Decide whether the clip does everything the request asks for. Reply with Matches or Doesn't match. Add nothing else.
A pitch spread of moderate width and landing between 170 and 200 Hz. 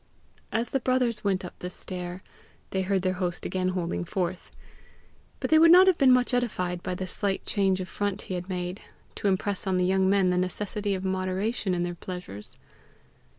Doesn't match